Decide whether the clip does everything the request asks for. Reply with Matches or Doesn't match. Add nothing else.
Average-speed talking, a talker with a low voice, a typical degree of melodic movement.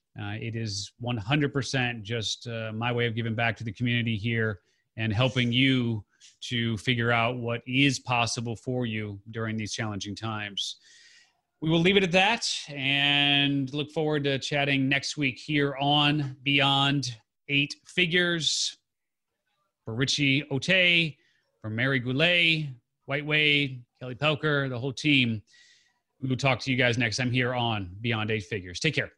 Matches